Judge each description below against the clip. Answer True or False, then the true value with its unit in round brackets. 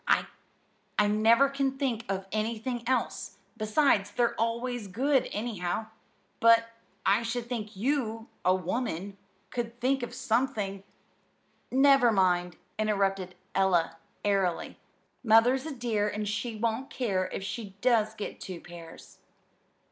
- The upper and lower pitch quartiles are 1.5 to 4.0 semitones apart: True (3.7 semitones)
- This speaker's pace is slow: True (125 wpm)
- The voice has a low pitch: False (220 Hz)